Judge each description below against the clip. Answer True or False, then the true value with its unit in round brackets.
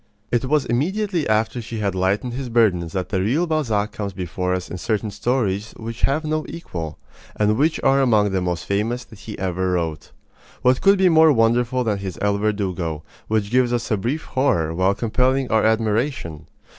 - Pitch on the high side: False (110 Hz)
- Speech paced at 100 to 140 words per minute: False (190 wpm)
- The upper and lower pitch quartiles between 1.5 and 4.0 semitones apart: False (5.1 semitones)